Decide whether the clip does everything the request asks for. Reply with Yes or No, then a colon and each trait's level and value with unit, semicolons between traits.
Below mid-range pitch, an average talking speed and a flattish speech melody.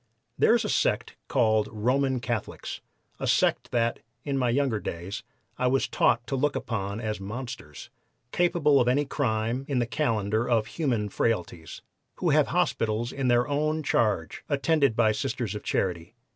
No: low, 120 Hz; average, 160 wpm; average, 4.0 semitones